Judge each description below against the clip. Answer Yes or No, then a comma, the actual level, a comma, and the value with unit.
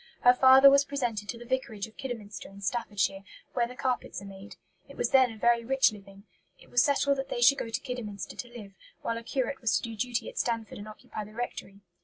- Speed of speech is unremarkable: No, fast, 235 wpm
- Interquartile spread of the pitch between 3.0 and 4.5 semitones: Yes, average, 3.6 semitones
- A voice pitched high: Yes, high, 235 Hz